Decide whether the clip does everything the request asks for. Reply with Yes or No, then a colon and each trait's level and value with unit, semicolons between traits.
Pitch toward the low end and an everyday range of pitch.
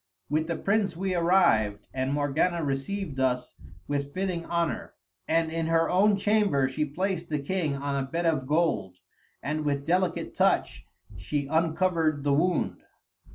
No: medium, 160 Hz; average, 4.1 semitones